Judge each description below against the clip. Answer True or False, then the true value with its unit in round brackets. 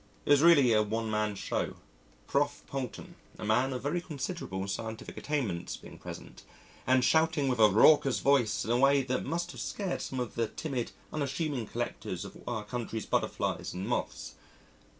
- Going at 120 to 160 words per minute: False (170 wpm)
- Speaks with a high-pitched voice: False (130 Hz)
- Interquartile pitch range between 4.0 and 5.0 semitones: True (4.7 semitones)